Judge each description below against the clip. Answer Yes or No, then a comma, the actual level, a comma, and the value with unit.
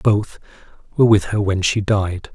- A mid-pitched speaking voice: No, low, 100 Hz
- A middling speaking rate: Yes, average, 180 wpm